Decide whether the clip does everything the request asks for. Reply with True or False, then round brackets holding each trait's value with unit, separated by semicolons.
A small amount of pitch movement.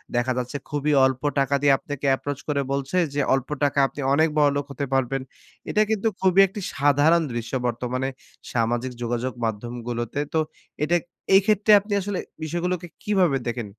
False (5.1 semitones)